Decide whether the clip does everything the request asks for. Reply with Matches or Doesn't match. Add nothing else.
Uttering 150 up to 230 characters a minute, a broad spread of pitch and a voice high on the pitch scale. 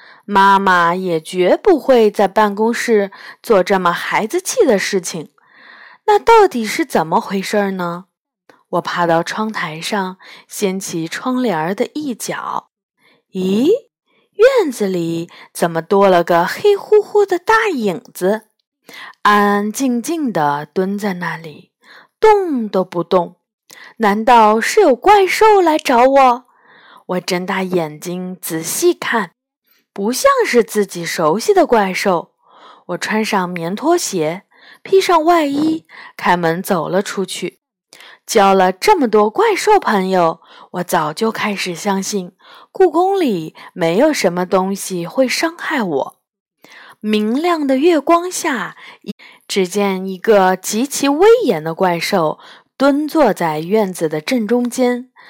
Matches